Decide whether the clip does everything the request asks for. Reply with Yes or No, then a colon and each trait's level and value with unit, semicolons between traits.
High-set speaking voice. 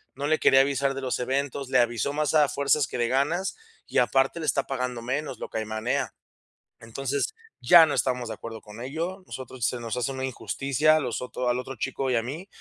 No: low, 135 Hz